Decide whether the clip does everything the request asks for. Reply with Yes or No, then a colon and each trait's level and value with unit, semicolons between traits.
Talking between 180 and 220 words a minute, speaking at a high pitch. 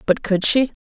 Yes: fast, 215 wpm; high, 215 Hz